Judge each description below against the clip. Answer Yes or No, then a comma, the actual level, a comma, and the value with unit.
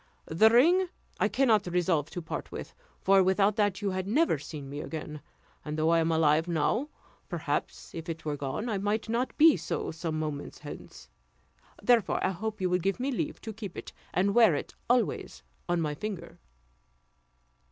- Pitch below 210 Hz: Yes, medium, 185 Hz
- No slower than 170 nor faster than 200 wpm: Yes, average, 185 wpm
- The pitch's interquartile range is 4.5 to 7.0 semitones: Yes, wide, 5.5 semitones